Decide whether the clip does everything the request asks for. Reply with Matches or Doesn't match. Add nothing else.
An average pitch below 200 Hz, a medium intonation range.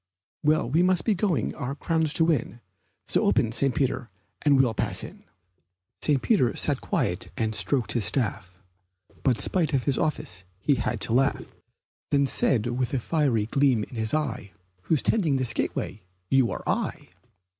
Matches